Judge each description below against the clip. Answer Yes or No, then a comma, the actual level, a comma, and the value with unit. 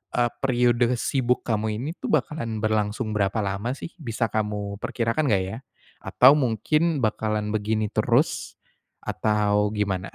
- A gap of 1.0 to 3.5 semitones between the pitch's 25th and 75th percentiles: Yes, average, 2.9 semitones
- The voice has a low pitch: Yes, low, 110 Hz